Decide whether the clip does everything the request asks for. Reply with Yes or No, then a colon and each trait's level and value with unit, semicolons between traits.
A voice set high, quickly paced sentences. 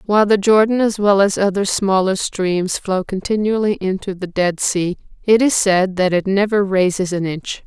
No: high, 195 Hz; average, 190 wpm